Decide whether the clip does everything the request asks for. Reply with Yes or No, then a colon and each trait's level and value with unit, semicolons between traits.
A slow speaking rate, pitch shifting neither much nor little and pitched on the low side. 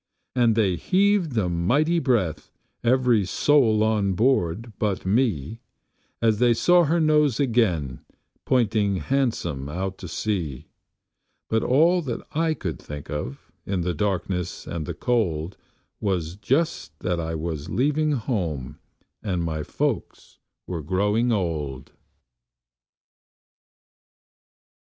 No: slow, 120 wpm; wide, 6.9 semitones; low, 105 Hz